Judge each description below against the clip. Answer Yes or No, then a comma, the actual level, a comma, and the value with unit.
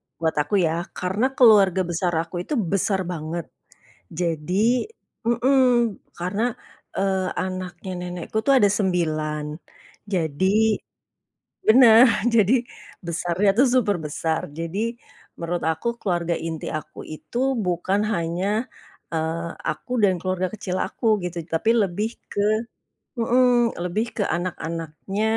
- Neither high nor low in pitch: Yes, medium, 180 Hz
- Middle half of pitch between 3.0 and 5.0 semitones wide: Yes, average, 3.7 semitones